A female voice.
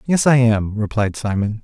No: male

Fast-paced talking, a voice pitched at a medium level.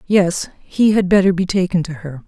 Yes: fast, 210 wpm; medium, 180 Hz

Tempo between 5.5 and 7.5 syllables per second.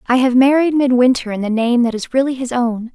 Yes: 5.8 syllables/s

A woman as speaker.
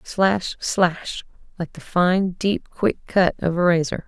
Yes: female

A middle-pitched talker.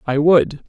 Yes: medium, 155 Hz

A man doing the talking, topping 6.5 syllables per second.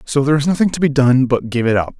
Yes: male; 7.0 syllables/s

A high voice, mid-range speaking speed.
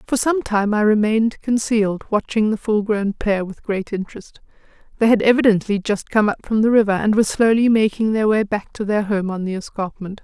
No: high, 210 Hz; fast, 210 wpm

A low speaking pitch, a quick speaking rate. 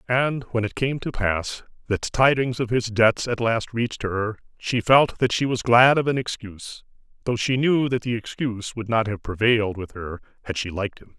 Yes: low, 115 Hz; fast, 215 wpm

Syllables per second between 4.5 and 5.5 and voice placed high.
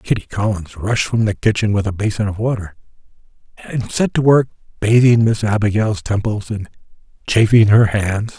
No: 5.0 syllables/s; low, 105 Hz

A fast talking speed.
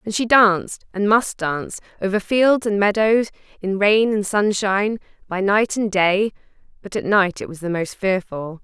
No: average, 180 wpm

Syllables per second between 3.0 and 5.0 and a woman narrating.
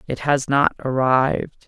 Yes: 4.4 syllables/s; female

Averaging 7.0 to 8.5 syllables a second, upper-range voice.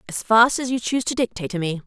Yes: 7.2 syllables/s; high, 220 Hz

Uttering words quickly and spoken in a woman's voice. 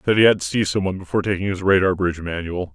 No: fast, 265 wpm; male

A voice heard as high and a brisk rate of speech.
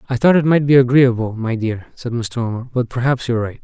No: low, 120 Hz; fast, 250 wpm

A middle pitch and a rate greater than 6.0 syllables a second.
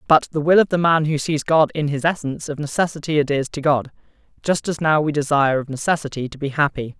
Yes: medium, 150 Hz; 6.4 syllables/s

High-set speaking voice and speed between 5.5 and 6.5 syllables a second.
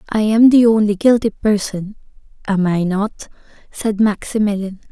No: high, 210 Hz; 4.5 syllables/s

